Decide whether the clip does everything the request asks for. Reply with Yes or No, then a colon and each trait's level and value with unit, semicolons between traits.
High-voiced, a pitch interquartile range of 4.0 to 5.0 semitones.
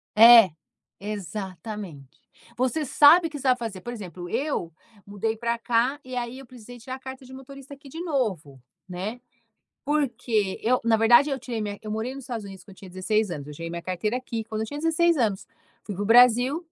Yes: high, 230 Hz; average, 4.5 semitones